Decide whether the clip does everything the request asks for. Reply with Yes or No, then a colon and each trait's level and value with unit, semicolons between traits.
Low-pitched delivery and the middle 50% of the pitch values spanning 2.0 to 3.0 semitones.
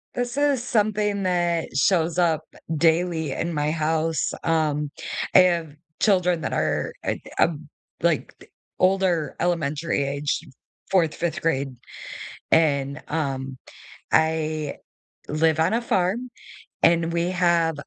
No: medium, 165 Hz; average, 2.7 semitones